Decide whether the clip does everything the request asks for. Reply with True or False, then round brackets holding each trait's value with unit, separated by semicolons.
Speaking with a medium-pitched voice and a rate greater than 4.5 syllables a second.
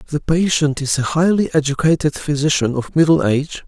True (150 Hz; 5.3 syllables/s)